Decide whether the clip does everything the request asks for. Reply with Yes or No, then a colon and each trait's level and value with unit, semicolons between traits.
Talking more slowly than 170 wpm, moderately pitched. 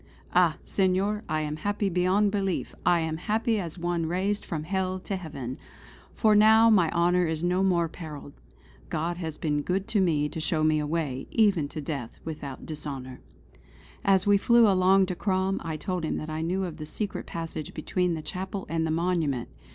No: average, 190 wpm; medium, 175 Hz